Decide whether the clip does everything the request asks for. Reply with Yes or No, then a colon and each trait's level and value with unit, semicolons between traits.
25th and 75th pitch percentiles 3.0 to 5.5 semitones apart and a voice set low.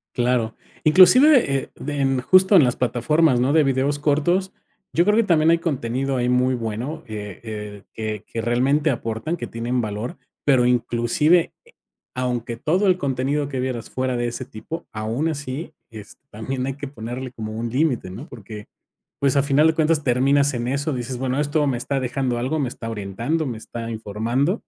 Yes: average, 4.0 semitones; low, 130 Hz